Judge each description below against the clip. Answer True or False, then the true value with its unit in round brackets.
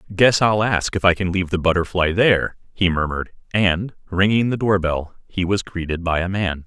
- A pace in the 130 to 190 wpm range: False (200 wpm)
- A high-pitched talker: False (95 Hz)